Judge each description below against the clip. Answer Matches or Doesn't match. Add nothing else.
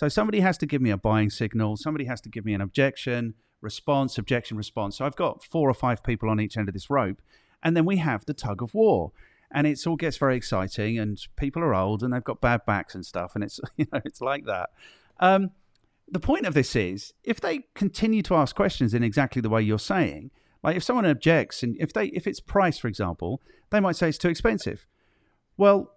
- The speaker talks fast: Matches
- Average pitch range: Doesn't match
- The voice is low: Matches